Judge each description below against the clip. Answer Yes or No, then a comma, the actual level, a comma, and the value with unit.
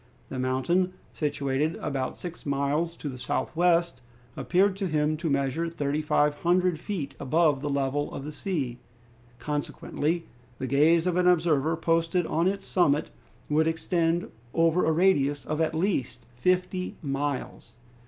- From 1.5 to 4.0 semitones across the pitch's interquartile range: Yes, average, 3.4 semitones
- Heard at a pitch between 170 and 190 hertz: No, medium, 160 Hz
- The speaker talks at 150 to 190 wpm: No, average, 140 wpm